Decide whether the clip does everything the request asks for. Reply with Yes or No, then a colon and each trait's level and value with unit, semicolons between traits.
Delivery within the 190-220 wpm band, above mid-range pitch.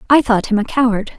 No: fast, 255 wpm; high, 230 Hz